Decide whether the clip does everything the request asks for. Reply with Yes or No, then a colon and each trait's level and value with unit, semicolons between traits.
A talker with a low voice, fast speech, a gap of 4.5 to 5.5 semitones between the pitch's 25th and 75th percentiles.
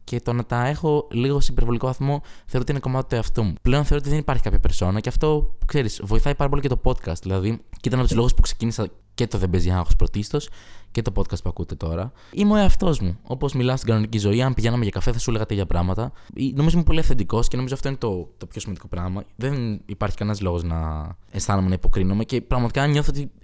Yes: low, 115 Hz; fast, 240 wpm; average, 4.9 semitones